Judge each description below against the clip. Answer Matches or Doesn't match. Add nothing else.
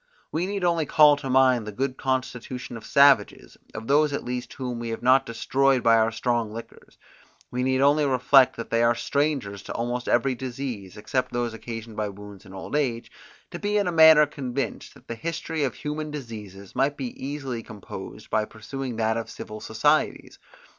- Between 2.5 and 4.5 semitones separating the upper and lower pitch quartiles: Matches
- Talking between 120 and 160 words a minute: Doesn't match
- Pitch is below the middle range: Matches